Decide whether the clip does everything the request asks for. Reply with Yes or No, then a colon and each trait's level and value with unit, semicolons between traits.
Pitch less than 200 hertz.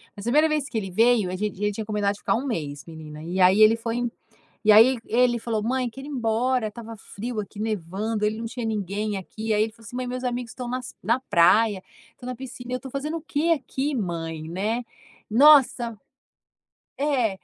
No: high, 225 Hz